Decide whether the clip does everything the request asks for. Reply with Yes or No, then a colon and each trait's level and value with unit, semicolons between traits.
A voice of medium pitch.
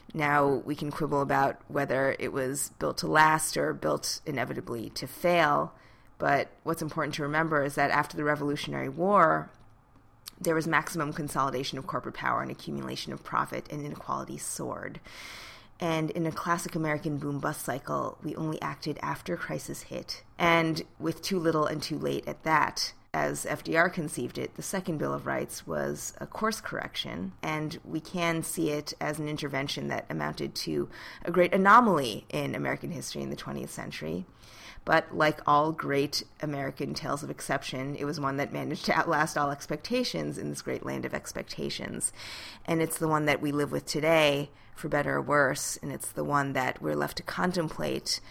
Yes: medium, 145 Hz